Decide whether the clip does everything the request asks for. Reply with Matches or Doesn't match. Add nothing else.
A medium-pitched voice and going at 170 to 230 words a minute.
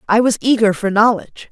Doesn't match